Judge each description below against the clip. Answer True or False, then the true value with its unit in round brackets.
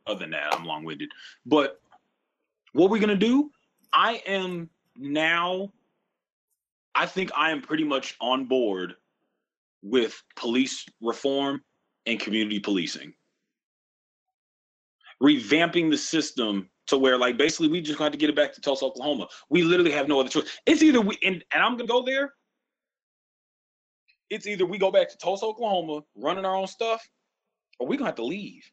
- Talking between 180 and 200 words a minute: False (160 wpm)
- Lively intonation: True (8.3 semitones)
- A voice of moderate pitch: True (175 Hz)